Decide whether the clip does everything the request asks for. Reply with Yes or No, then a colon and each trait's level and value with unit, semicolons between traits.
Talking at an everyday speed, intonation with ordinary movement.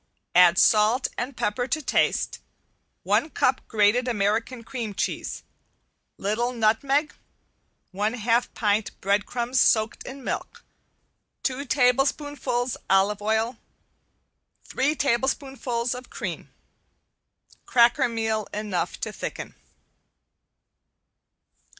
No: slow, 95 wpm; average, 3.2 semitones